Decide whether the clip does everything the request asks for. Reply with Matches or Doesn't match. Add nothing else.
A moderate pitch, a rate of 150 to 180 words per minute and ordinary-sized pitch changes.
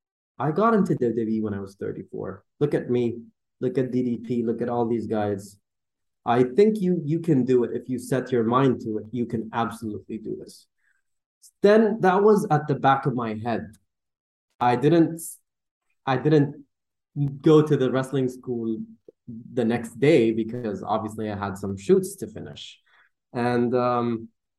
Doesn't match